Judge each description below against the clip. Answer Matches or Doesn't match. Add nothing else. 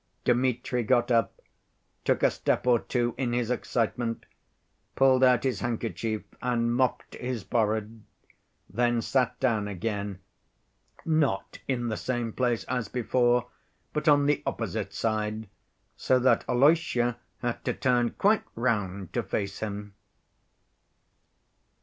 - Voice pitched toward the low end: Matches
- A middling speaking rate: Doesn't match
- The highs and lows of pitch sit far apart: Doesn't match